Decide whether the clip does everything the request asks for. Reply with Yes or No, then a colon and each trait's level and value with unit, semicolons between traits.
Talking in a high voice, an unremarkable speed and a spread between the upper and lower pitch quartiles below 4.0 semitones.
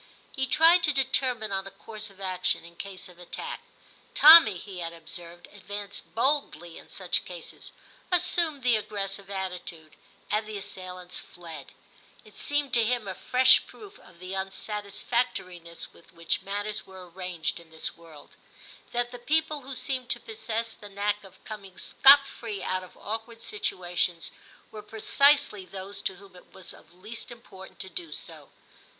No: high, 200 Hz; average, 160 wpm; average, 4.8 semitones